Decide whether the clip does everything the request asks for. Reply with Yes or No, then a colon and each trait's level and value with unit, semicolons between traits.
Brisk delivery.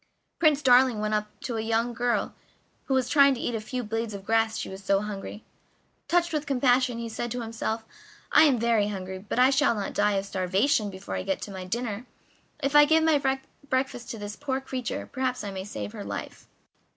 Yes: fast, 210 wpm